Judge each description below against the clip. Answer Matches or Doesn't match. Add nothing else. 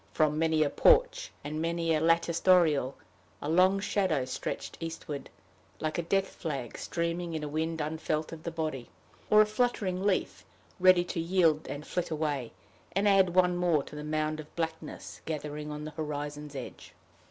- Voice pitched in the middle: Matches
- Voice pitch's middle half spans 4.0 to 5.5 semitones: Doesn't match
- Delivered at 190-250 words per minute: Doesn't match